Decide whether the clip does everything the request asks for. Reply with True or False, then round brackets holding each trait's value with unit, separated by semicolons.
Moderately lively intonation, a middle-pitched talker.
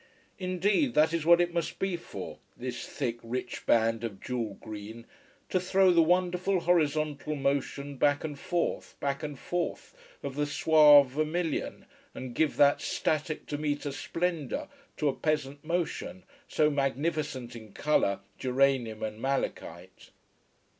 True (4.4 semitones; 145 Hz)